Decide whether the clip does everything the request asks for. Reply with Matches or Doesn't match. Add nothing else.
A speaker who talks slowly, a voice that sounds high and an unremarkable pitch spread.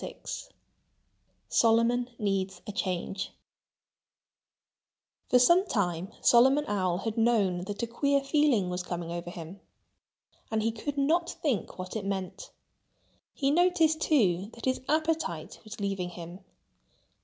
Doesn't match